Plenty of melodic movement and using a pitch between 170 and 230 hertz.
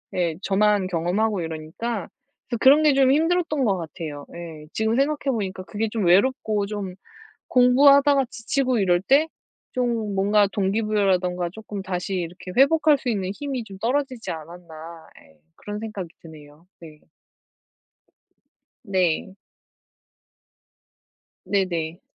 Yes: wide, 5.8 semitones; high, 200 Hz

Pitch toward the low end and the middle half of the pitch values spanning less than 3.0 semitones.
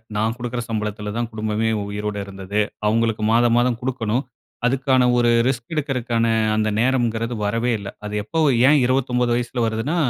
Yes: low, 115 Hz; narrow, 2.4 semitones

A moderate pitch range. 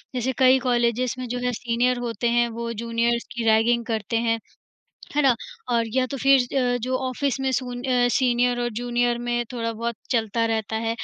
No: narrow, 1.3 semitones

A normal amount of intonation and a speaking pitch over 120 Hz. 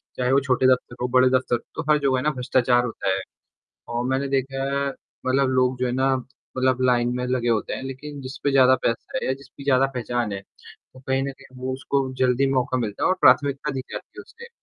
No: narrow, 1.4 semitones; low, 130 Hz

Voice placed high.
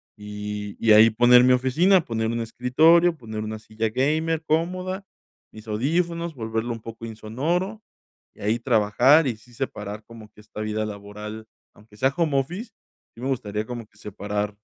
No: low, 115 Hz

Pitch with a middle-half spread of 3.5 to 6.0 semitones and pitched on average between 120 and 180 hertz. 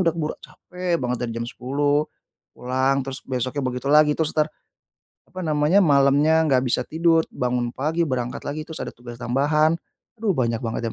Yes: average, 3.8 semitones; medium, 140 Hz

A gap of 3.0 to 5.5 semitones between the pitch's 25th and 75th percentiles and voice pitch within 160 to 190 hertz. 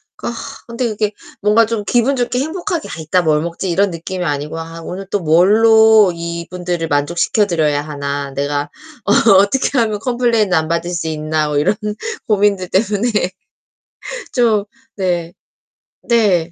Yes: average, 5.2 semitones; medium, 185 Hz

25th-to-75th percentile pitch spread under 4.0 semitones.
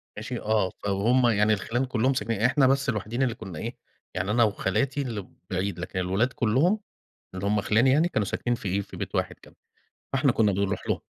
No: average, 4.4 semitones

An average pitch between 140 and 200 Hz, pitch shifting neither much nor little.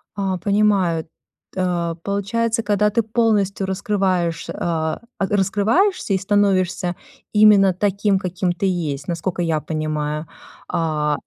Yes: high, 190 Hz; average, 3.3 semitones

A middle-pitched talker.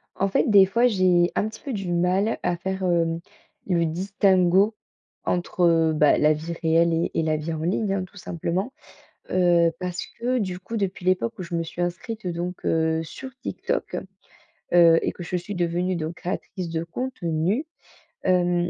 Yes: medium, 175 Hz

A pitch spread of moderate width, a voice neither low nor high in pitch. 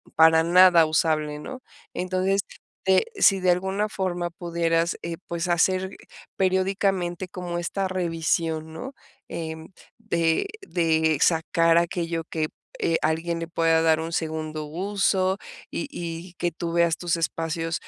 No: narrow, 2.2 semitones; medium, 170 Hz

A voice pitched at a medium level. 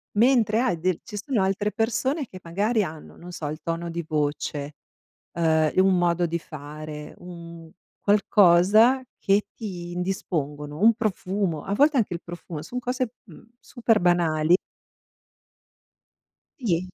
Yes: medium, 180 Hz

